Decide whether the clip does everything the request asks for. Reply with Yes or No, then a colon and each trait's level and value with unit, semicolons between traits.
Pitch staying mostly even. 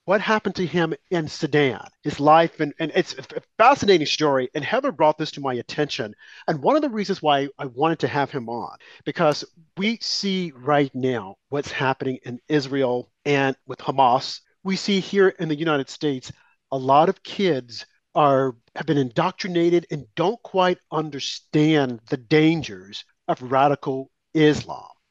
No: average, 4.2 semitones